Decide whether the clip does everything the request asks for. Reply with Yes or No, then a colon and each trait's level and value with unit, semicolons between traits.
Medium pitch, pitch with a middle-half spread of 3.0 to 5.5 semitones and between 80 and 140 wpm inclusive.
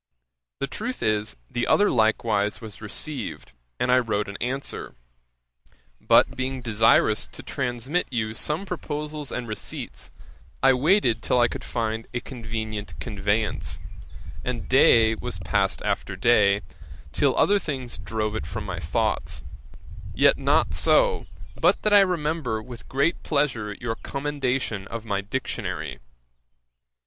No: low, 120 Hz; average, 4.3 semitones; slow, 135 wpm